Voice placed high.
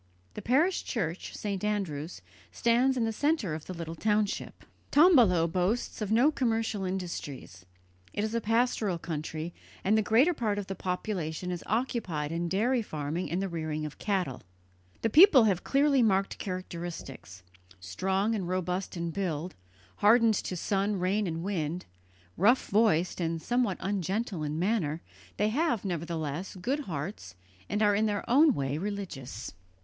Yes: high, 195 Hz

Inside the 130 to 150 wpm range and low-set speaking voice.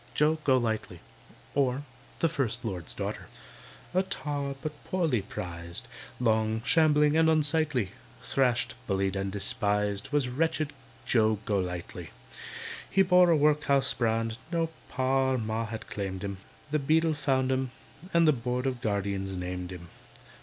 Yes: average, 140 wpm; low, 125 Hz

